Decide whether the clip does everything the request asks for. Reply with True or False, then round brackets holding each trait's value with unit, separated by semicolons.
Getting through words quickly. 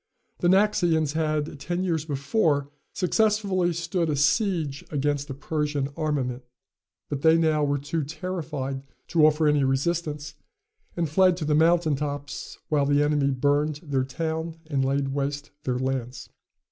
False (145 wpm)